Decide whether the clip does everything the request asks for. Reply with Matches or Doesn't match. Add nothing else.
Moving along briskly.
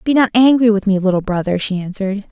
Matches